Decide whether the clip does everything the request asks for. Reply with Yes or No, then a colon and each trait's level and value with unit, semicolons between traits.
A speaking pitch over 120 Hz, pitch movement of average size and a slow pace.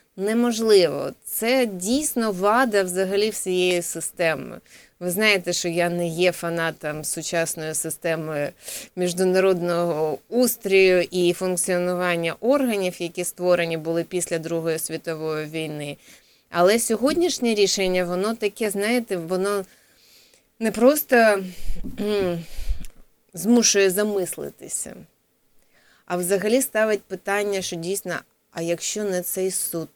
Yes: medium, 185 Hz; average, 3.5 semitones; slow, 100 wpm